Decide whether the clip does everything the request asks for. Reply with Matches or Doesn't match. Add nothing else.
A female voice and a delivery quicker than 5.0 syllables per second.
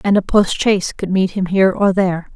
Matches